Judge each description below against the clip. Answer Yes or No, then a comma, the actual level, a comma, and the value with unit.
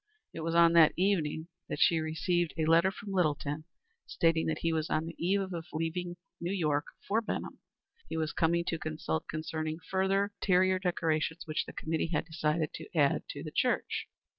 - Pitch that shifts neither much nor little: No, narrow, 2.2 semitones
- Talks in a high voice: No, medium, 165 Hz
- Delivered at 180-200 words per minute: Yes, average, 190 wpm